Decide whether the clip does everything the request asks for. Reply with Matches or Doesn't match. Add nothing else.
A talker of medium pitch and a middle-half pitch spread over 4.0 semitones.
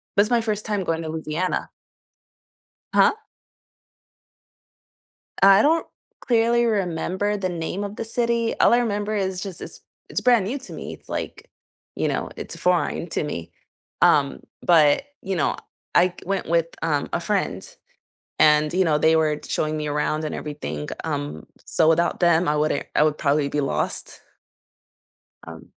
Matches